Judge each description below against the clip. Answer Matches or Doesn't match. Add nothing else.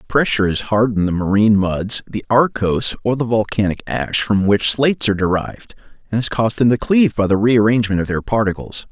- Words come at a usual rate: Matches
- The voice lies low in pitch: Matches